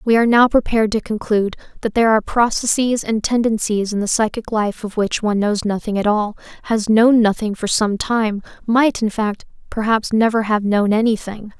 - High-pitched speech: Yes, high, 220 Hz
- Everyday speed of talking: Yes, average, 190 wpm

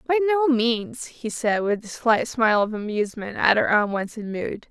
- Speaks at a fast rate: No, average, 190 wpm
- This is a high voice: Yes, high, 230 Hz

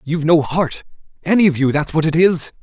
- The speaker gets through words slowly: No, fast, 205 wpm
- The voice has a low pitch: No, medium, 160 Hz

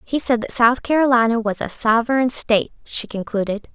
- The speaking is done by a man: No, female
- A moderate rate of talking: Yes, average, 175 wpm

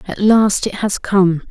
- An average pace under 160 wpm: No, average, 200 wpm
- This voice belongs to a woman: Yes, female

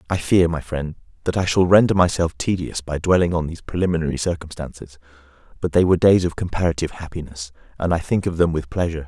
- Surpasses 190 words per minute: Yes, average, 200 wpm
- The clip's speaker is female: No, male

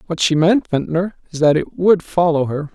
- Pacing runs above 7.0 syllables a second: No, 4.9 syllables/s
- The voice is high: No, medium, 165 Hz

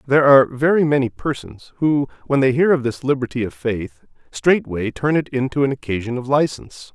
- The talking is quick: No, average, 190 wpm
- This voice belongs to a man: Yes, male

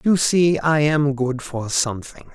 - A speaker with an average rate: Yes, average, 180 wpm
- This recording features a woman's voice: No, male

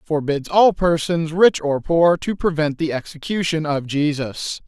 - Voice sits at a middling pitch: Yes, medium, 160 Hz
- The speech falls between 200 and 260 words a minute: No, average, 155 wpm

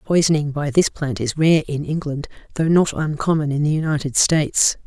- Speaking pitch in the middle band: Yes, medium, 150 Hz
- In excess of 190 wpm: No, average, 185 wpm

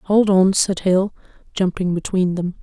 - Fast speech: No, average, 160 wpm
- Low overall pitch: No, medium, 185 Hz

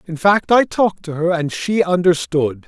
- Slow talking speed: No, average, 200 wpm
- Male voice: Yes, male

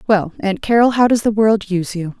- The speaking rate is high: Yes, fast, 245 wpm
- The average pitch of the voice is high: Yes, high, 205 Hz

